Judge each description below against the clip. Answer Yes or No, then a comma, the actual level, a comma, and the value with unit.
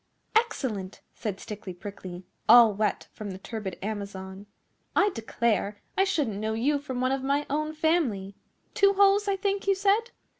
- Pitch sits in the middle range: No, high, 235 Hz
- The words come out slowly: No, average, 160 wpm